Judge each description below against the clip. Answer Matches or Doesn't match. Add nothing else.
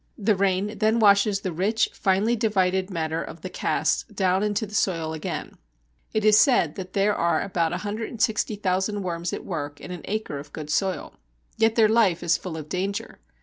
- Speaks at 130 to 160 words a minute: Doesn't match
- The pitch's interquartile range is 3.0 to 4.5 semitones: Matches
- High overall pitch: Matches